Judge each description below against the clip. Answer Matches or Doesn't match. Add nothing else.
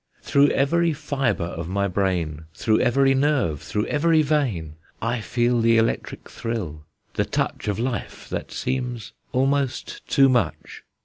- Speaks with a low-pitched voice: Matches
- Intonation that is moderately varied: Doesn't match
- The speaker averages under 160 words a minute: Matches